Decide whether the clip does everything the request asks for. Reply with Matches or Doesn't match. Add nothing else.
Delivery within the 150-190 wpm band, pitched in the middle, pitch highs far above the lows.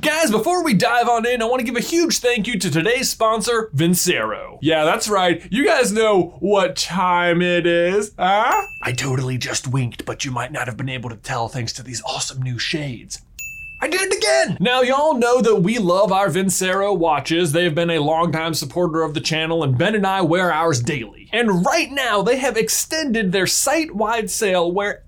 Doesn't match